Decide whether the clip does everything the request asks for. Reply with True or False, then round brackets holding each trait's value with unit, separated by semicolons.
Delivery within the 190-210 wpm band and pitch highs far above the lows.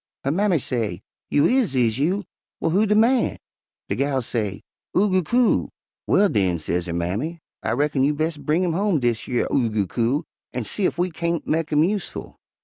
True (195 wpm; 7.6 semitones)